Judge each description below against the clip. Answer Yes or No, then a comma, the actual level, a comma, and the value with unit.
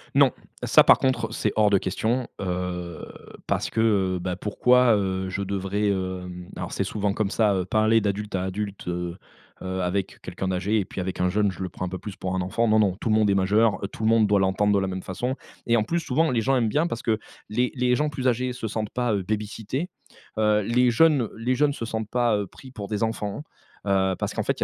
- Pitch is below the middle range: Yes, low, 105 Hz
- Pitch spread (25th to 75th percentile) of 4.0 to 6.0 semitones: No, average, 3.6 semitones